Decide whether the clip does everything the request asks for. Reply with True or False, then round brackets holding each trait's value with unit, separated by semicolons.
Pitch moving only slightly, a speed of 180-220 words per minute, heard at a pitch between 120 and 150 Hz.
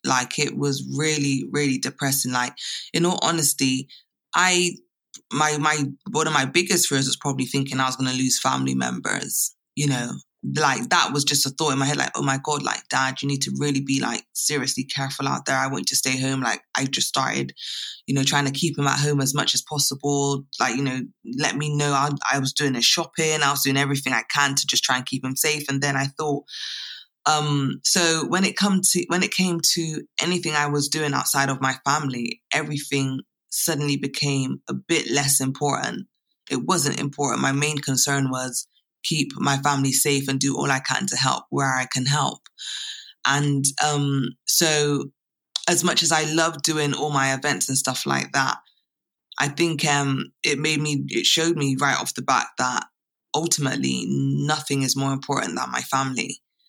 True (2.0 semitones; 200 wpm; 140 Hz)